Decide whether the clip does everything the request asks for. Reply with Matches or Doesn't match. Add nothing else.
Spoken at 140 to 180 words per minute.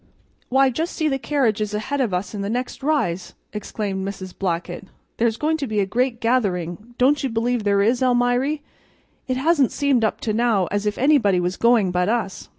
Doesn't match